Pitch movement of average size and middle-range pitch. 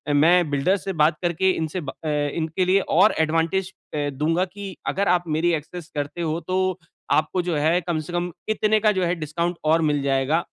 Yes: average, 3.0 semitones; medium, 170 Hz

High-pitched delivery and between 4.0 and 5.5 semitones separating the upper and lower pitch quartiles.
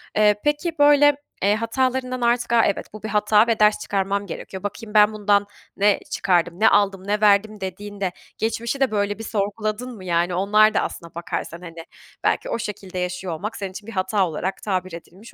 No: high, 205 Hz; average, 2.7 semitones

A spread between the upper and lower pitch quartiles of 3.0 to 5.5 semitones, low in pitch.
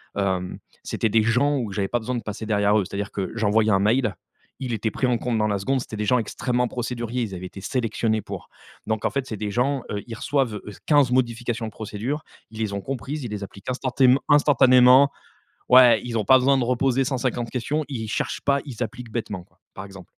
Yes: average, 3.4 semitones; low, 115 Hz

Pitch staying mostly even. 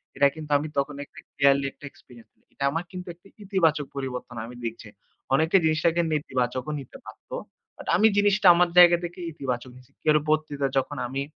No: average, 4.1 semitones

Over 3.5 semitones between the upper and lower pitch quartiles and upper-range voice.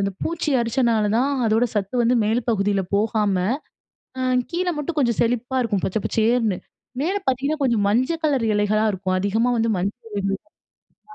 Yes: average, 3.9 semitones; high, 230 Hz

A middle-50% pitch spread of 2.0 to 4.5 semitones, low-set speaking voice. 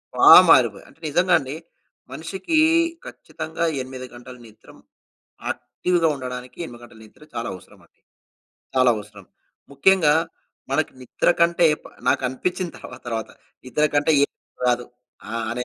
No: average, 5.0 semitones; low, 130 Hz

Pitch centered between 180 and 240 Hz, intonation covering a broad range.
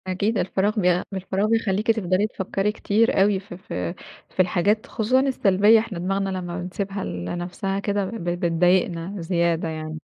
No: high, 190 Hz; average, 2.8 semitones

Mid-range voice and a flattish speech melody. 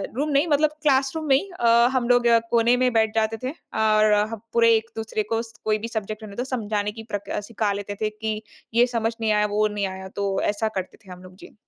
No: high, 220 Hz; narrow, 2.3 semitones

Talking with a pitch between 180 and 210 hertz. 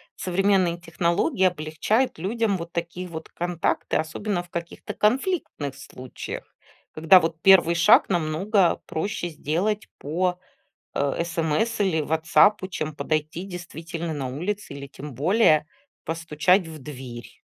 No: medium, 170 Hz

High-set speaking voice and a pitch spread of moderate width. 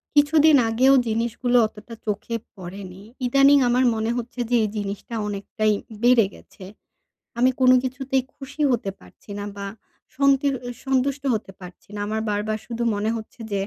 Yes: high, 235 Hz; average, 4.0 semitones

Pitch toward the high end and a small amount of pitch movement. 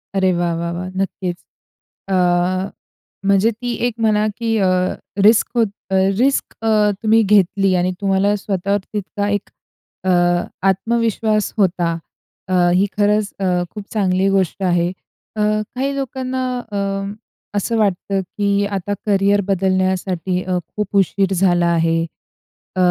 Yes: high, 200 Hz; narrow, 2.3 semitones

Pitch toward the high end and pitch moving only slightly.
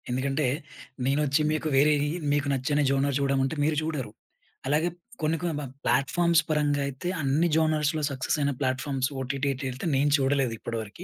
No: medium, 140 Hz; narrow, 2.2 semitones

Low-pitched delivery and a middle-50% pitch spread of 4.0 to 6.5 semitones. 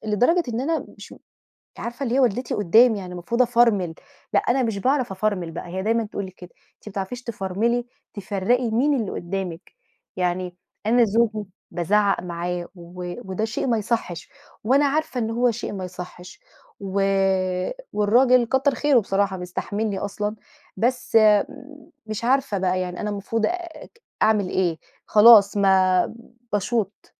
No: high, 210 Hz; average, 4.3 semitones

